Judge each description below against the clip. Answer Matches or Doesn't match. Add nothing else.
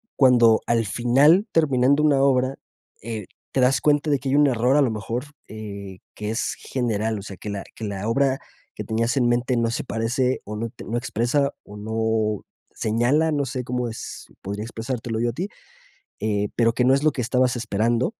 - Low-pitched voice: Matches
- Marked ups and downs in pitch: Doesn't match